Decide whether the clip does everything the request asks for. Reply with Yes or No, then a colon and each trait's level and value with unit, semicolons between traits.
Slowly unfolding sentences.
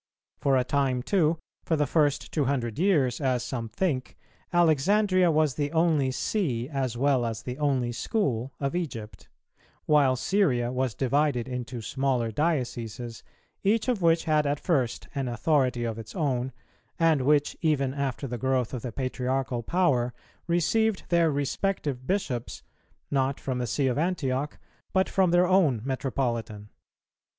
No: average, 150 wpm